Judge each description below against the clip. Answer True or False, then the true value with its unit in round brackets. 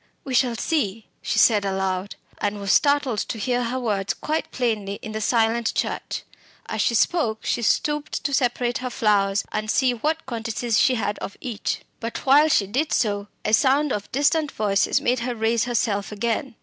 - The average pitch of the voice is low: False (230 Hz)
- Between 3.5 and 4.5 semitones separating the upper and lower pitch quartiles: True (3.8 semitones)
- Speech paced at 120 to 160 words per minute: False (185 wpm)